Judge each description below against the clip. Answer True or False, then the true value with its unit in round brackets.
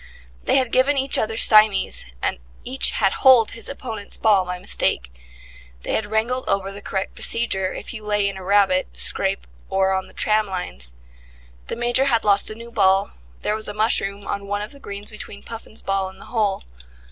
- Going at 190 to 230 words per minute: True (195 wpm)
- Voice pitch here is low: False (205 Hz)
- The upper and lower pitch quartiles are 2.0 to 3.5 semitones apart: True (2.9 semitones)